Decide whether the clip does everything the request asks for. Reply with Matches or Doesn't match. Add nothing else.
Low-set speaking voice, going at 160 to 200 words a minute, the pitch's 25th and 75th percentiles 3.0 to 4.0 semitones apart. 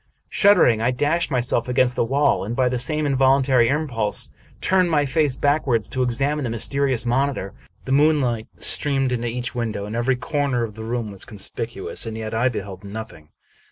Matches